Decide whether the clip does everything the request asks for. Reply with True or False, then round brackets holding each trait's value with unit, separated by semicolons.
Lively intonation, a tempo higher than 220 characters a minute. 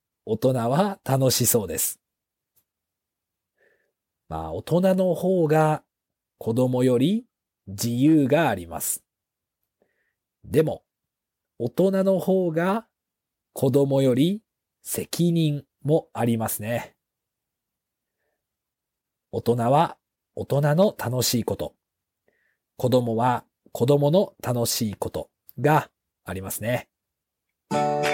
False (6.1 semitones; 160 characters per minute)